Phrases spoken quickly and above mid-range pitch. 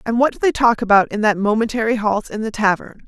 Yes: fast, 255 wpm; high, 220 Hz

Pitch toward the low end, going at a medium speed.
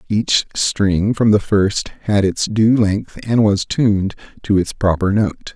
Yes: low, 105 Hz; average, 175 wpm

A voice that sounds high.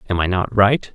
No: low, 100 Hz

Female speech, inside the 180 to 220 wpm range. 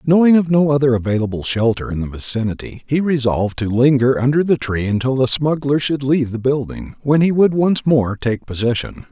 No: male; average, 195 wpm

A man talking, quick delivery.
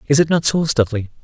Yes: male; fast, 245 wpm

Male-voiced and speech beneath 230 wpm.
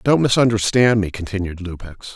Yes: male; average, 140 wpm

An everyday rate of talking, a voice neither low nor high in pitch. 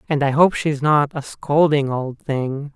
Yes: average, 195 wpm; medium, 145 Hz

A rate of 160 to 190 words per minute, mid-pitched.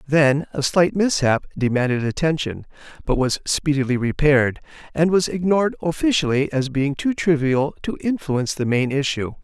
No: average, 145 wpm; medium, 145 Hz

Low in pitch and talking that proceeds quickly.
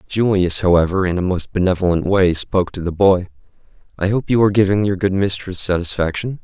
No: very low, 95 Hz; average, 175 wpm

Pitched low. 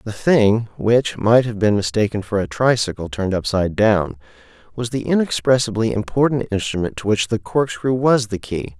Yes: low, 110 Hz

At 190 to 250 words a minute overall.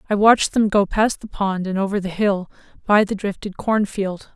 Yes: fast, 205 wpm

